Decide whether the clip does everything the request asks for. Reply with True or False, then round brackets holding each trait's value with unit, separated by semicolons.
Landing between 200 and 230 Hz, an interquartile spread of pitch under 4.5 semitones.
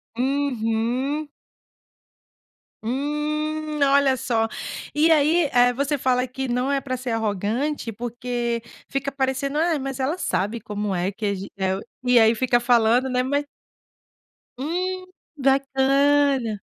False (260 Hz; 3.3 semitones)